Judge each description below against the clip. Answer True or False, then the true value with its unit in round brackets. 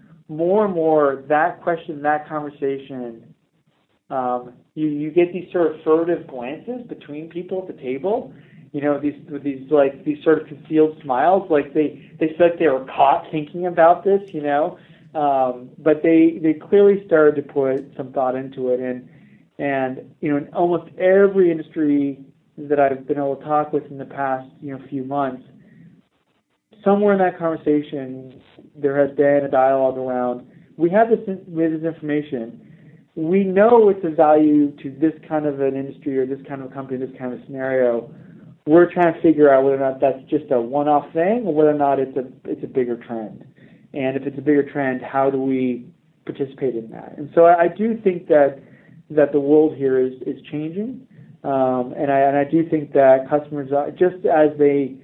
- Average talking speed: True (190 wpm)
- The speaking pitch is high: False (150 Hz)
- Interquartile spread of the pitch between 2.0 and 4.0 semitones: True (3.3 semitones)